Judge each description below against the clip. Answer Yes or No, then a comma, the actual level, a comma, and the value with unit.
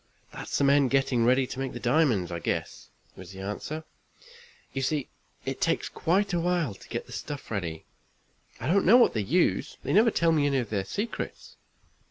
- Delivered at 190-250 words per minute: Yes, average, 195 wpm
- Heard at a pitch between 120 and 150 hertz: Yes, low, 135 Hz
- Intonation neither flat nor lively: No, wide, 7.2 semitones